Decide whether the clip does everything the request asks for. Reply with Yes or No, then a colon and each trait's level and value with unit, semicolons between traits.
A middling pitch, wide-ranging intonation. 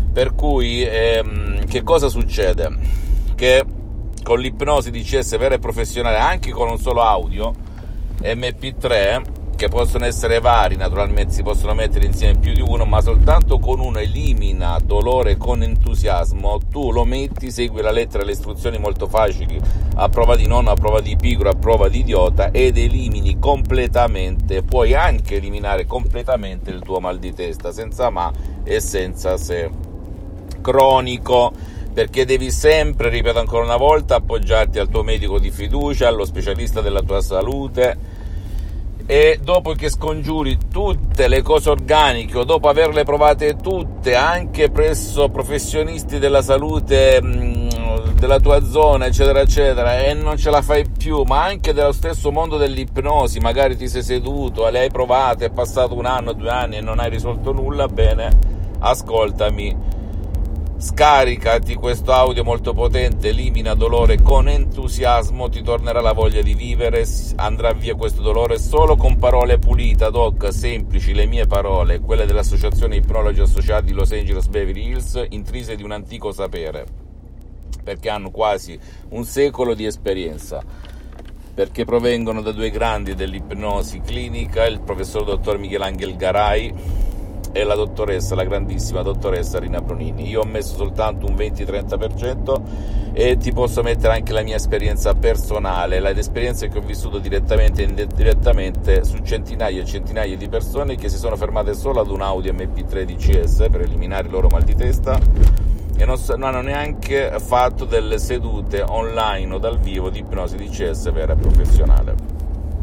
No: low, 100 Hz; wide, 5.7 semitones